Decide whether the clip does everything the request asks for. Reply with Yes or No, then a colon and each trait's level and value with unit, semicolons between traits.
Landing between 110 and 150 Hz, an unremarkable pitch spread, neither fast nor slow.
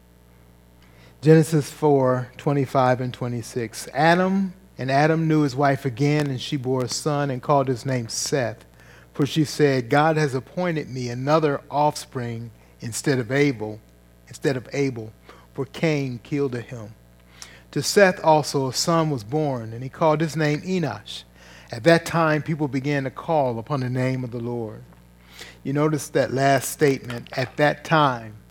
Yes: low, 135 Hz; average, 4.5 semitones; average, 160 wpm